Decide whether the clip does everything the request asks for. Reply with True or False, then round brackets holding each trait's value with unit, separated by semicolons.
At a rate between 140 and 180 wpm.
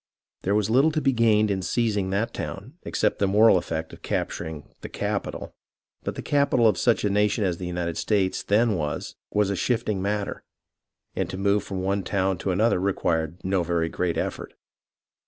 False (190 wpm)